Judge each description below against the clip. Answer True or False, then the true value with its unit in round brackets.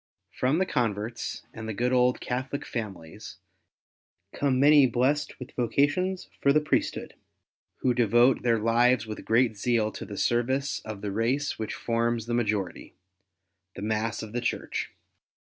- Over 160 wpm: False (155 wpm)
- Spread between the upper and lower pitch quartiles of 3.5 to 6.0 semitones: False (3.0 semitones)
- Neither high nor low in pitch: False (120 Hz)